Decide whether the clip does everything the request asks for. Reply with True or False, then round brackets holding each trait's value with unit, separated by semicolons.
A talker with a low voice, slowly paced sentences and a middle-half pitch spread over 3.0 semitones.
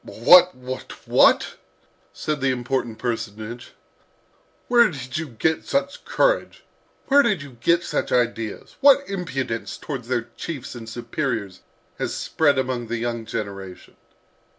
True (130 Hz; 130 wpm; 5.6 semitones)